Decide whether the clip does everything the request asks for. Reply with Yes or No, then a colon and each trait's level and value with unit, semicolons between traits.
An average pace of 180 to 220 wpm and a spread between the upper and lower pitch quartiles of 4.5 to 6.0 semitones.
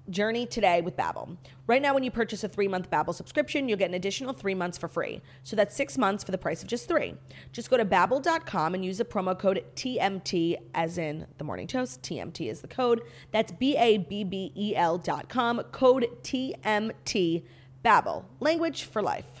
Yes: average, 200 wpm; wide, 5.5 semitones